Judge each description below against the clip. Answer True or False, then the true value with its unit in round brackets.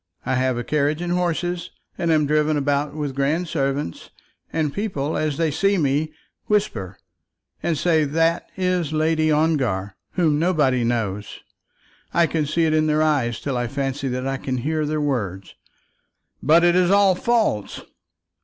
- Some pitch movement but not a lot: True (3.6 semitones)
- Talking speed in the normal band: True (165 wpm)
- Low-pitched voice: False (150 Hz)